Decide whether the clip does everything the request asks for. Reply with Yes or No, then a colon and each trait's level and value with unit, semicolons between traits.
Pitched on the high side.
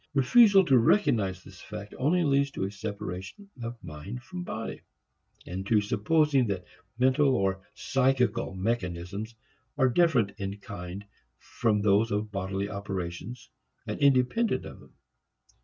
No: low, 110 Hz